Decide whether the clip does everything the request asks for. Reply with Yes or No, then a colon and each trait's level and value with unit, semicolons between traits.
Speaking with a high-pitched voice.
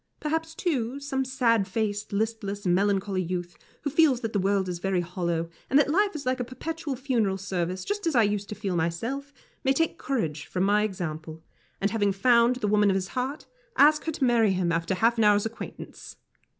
Yes: high, 210 Hz